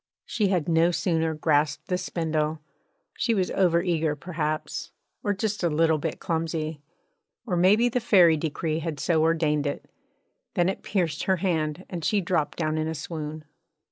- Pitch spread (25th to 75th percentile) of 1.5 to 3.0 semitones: Yes, average, 2.7 semitones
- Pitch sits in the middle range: Yes, medium, 165 Hz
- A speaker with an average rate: Yes, average, 170 wpm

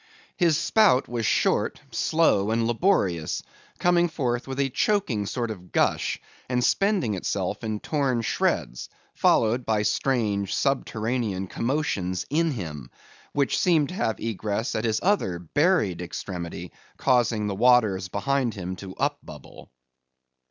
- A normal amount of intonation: No, wide, 5.9 semitones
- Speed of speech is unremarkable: No, slow, 130 wpm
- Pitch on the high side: No, low, 115 Hz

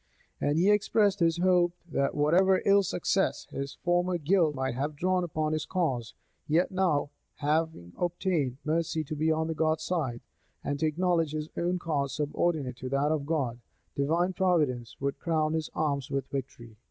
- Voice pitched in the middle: Yes, medium, 155 Hz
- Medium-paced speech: Yes, average, 165 wpm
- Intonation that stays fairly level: No, average, 3.7 semitones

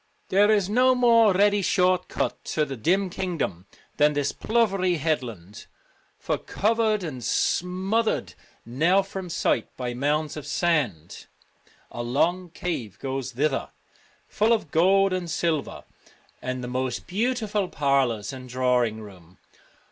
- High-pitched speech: No, medium, 165 Hz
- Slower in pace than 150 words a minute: Yes, average, 140 wpm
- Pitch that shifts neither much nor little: No, wide, 7.3 semitones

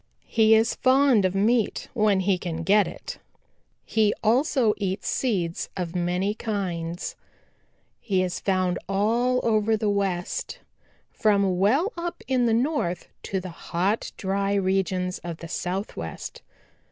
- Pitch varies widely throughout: No, average, 3.6 semitones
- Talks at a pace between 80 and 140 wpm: Yes, slow, 135 wpm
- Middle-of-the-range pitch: No, high, 200 Hz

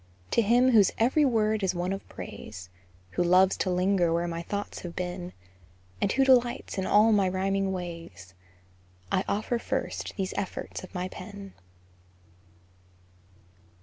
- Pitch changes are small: No, average, 3.1 semitones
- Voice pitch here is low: No, high, 190 Hz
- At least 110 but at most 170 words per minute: Yes, average, 150 wpm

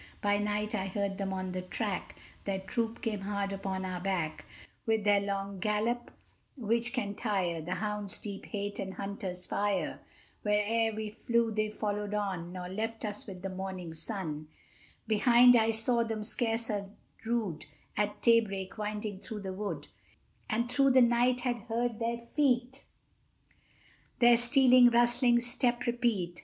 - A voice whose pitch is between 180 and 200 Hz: No, high, 210 Hz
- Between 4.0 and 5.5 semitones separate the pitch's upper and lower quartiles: No, average, 3.2 semitones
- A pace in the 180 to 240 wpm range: No, average, 155 wpm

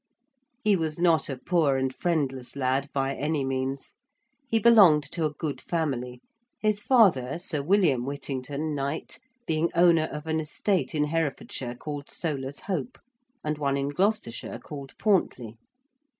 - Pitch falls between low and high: Yes, medium, 150 Hz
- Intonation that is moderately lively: Yes, average, 3.9 semitones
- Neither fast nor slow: Yes, average, 145 wpm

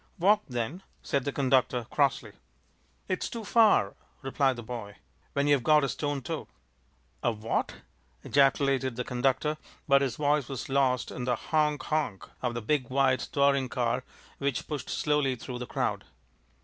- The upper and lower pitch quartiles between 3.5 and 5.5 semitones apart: No, average, 2.7 semitones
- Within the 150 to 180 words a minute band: Yes, average, 160 wpm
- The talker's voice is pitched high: No, low, 135 Hz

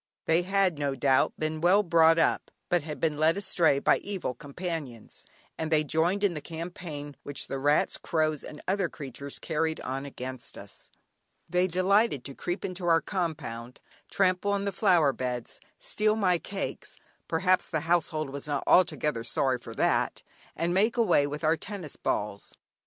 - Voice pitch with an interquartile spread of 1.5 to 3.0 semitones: No, average, 4.2 semitones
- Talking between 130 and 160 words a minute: No, average, 170 wpm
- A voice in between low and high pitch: Yes, medium, 160 Hz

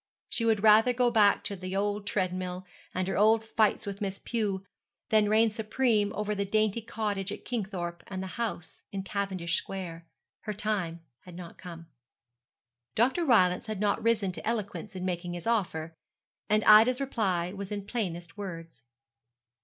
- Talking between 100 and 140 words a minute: No, average, 165 wpm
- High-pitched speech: Yes, high, 200 Hz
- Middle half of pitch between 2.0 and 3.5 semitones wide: Yes, average, 3.0 semitones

